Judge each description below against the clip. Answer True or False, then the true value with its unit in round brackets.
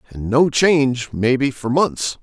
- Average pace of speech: True (160 wpm)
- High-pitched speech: False (130 Hz)